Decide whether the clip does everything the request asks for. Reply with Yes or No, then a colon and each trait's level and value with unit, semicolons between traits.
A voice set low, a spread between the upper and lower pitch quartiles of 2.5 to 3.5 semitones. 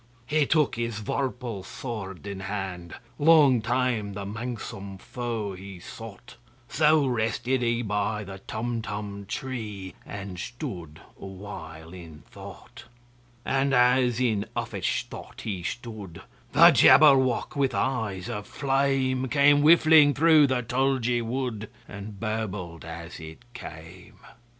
No: low, 115 Hz; average, 4.7 semitones